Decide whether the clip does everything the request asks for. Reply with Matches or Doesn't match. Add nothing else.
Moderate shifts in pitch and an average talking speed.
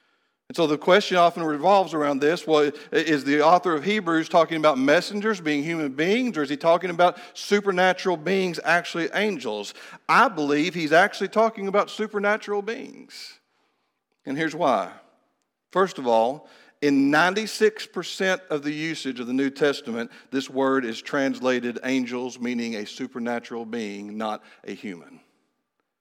Doesn't match